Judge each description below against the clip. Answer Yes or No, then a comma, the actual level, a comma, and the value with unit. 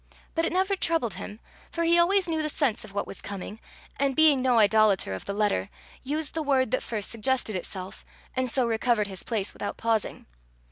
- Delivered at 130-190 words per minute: No, average, 200 wpm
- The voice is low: No, high, 235 Hz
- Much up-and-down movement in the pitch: Yes, wide, 6.8 semitones